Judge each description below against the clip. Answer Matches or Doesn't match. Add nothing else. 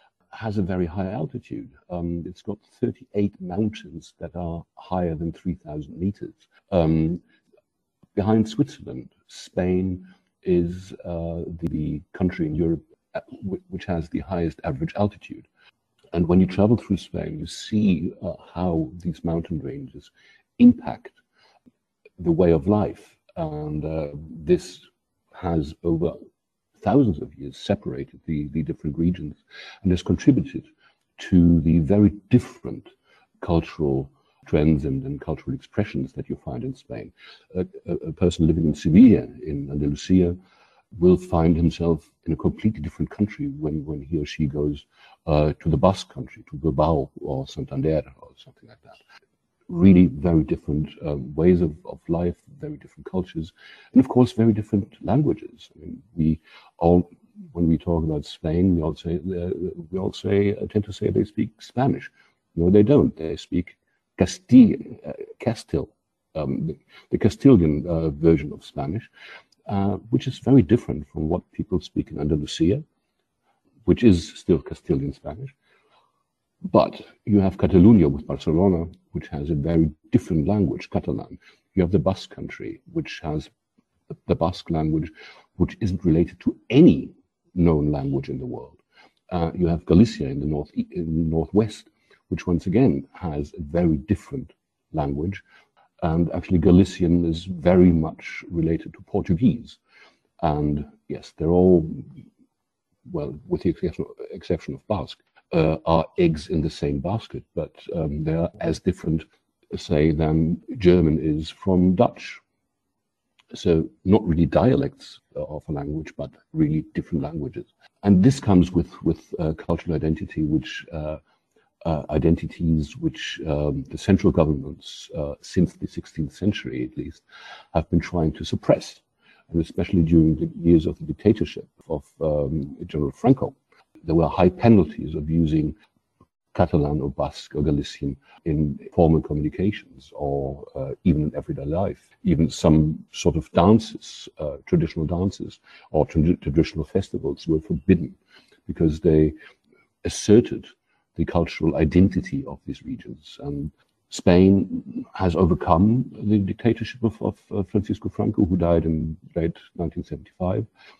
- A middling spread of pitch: Matches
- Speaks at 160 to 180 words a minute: Doesn't match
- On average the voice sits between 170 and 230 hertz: Doesn't match